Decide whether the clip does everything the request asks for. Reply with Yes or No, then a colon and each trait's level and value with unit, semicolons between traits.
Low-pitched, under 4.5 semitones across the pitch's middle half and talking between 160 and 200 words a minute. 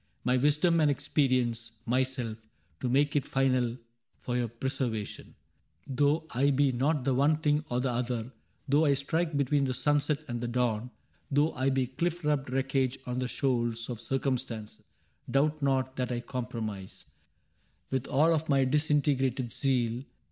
Yes: low, 130 Hz; average, 2.8 semitones; average, 165 wpm